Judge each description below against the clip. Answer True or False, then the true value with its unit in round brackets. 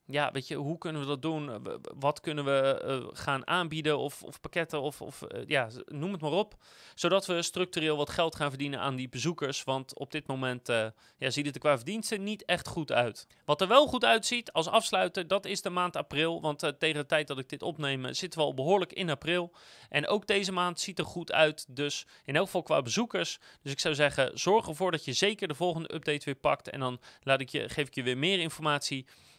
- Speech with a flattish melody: False (4.1 semitones)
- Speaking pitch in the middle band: True (155 Hz)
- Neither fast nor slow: False (235 wpm)